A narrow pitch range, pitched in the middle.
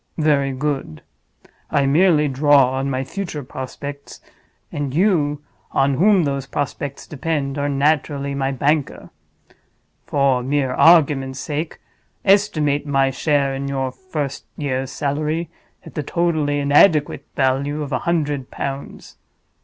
Yes: narrow, 1.9 semitones; medium, 145 Hz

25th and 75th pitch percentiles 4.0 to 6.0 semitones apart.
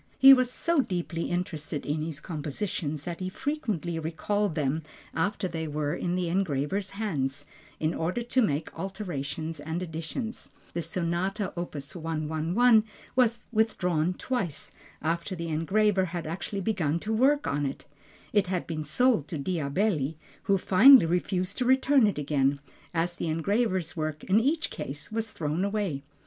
Yes: average, 5.0 semitones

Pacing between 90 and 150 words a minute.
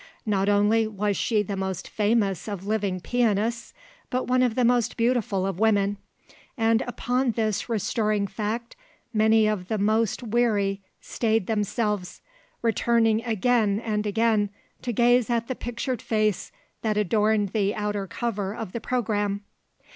Yes: average, 145 wpm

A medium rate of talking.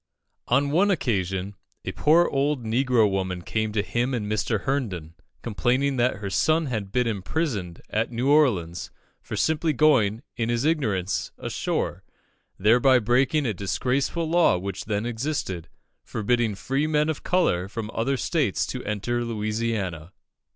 Yes: average, 145 wpm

